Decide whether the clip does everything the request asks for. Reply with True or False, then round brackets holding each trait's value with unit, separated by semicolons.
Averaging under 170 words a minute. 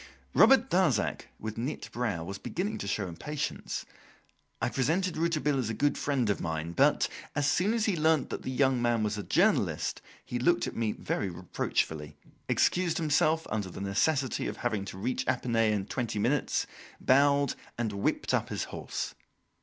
False (175 wpm)